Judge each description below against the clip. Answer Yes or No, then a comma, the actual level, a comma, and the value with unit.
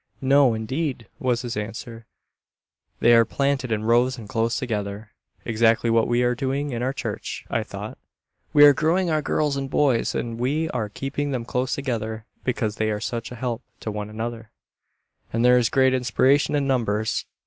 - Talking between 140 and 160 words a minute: No, average, 180 wpm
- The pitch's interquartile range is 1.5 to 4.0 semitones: Yes, average, 3.2 semitones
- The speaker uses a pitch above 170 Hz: No, low, 120 Hz